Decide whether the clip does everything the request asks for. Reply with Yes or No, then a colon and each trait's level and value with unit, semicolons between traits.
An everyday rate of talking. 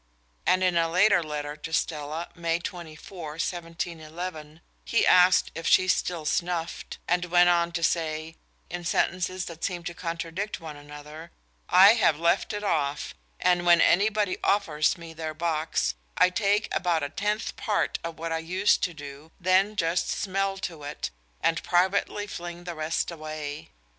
Yes: average, 160 wpm